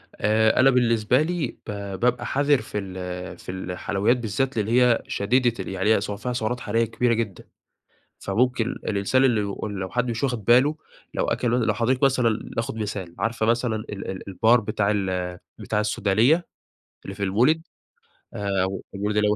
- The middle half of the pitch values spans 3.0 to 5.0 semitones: Yes, average, 3.5 semitones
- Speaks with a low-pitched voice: Yes, low, 110 Hz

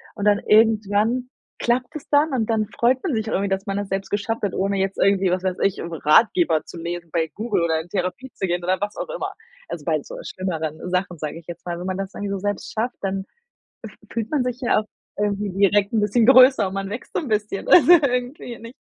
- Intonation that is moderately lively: Yes, average, 4.0 semitones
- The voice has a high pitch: Yes, high, 205 Hz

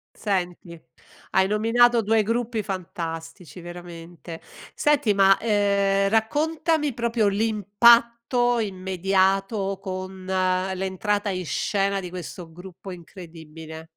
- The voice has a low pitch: No, high, 195 Hz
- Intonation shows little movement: No, average, 3.4 semitones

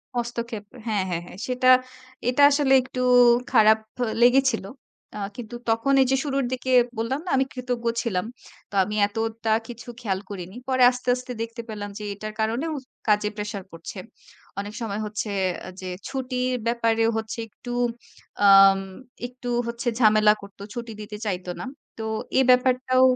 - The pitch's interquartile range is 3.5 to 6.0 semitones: No, average, 3.1 semitones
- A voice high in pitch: Yes, high, 230 Hz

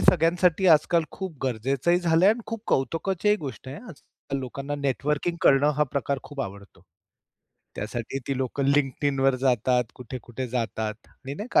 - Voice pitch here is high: No, medium, 140 Hz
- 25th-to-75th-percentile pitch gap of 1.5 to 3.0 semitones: No, average, 4.4 semitones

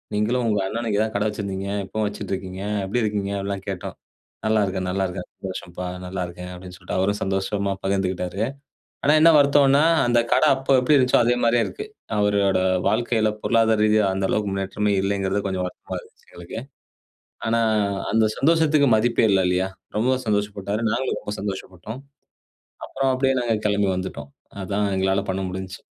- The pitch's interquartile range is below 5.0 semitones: Yes, average, 3.3 semitones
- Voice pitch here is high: No, low, 100 Hz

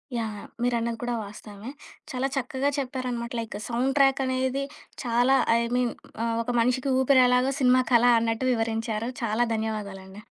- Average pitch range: No, narrow, 2.3 semitones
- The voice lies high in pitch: Yes, high, 240 Hz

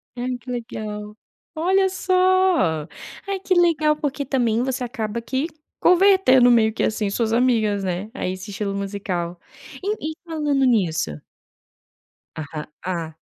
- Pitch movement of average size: No, wide, 7.2 semitones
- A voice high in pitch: Yes, high, 240 Hz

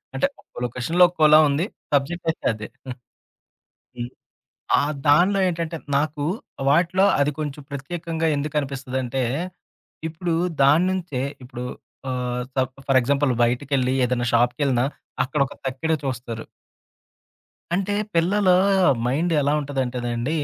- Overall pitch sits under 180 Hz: Yes, medium, 140 Hz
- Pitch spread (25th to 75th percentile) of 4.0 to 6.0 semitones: Yes, average, 4.4 semitones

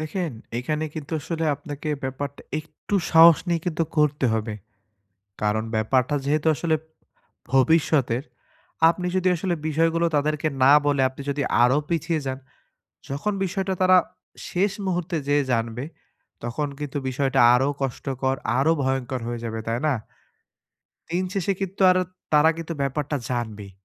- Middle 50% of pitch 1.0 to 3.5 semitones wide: No, average, 3.9 semitones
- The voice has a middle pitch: Yes, medium, 145 Hz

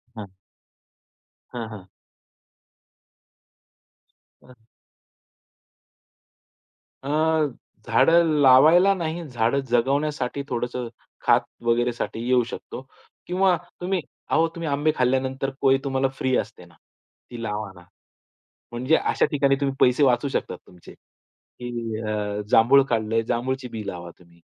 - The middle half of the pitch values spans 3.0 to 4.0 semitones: Yes, average, 3.6 semitones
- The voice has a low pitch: Yes, low, 130 Hz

